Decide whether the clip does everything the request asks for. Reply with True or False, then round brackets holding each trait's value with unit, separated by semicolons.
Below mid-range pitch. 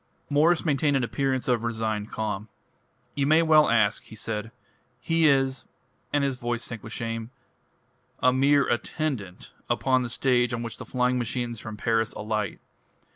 True (120 Hz)